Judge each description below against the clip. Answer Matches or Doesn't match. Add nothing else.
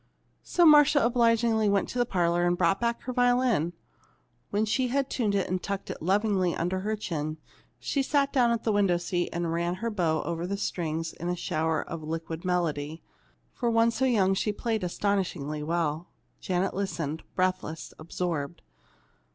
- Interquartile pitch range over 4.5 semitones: Matches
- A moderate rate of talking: Matches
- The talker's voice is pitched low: Doesn't match